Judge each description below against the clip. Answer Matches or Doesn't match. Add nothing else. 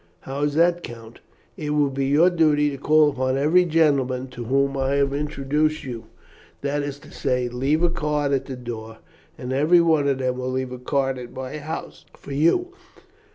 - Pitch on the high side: Doesn't match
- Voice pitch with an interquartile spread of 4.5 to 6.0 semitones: Doesn't match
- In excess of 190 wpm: Matches